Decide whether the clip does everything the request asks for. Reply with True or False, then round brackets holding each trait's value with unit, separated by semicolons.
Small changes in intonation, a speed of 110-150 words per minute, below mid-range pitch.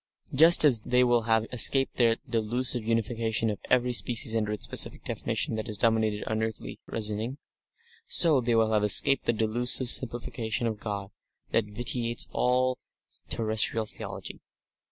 True (2.2 semitones; 145 wpm; 115 Hz)